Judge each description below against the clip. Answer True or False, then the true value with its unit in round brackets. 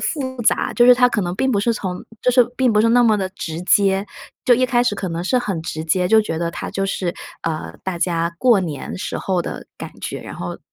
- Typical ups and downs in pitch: False (5.7 semitones)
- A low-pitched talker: False (195 Hz)